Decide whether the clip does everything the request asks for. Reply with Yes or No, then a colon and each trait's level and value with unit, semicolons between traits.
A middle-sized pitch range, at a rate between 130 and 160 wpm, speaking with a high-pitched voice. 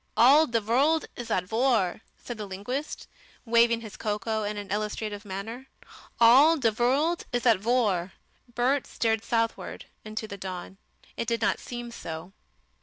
Yes: average, 3.0 semitones; average, 155 wpm; high, 225 Hz